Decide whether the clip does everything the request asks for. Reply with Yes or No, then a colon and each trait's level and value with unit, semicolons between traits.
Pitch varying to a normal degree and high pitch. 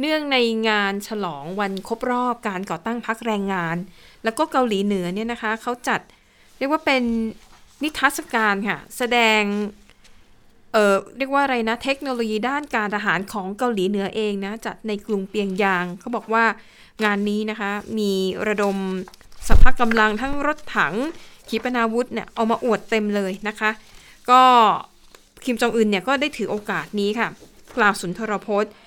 Yes: average, 3.0 semitones; high, 220 Hz